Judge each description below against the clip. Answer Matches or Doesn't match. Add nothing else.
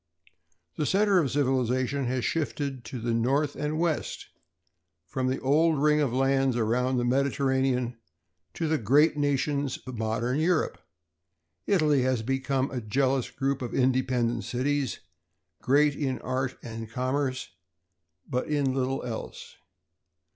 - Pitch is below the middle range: Matches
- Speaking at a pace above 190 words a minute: Doesn't match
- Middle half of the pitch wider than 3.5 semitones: Doesn't match